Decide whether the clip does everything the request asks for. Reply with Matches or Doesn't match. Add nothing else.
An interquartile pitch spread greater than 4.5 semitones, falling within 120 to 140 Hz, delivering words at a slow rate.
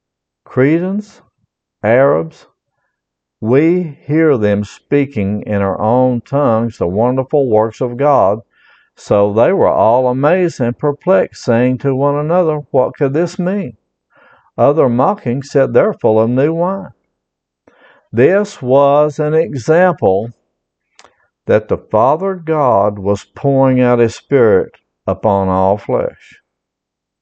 Matches